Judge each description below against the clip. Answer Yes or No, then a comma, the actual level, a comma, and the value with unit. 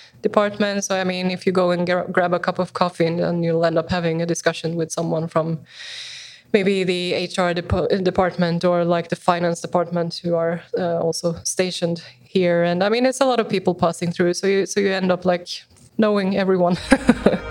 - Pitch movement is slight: Yes, narrow, 2.2 semitones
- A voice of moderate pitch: Yes, medium, 180 Hz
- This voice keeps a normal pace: No, fast, 205 wpm